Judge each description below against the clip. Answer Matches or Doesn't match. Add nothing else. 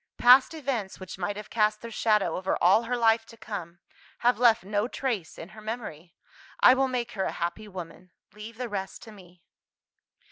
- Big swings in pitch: Doesn't match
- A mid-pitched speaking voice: Doesn't match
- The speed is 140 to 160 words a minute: Doesn't match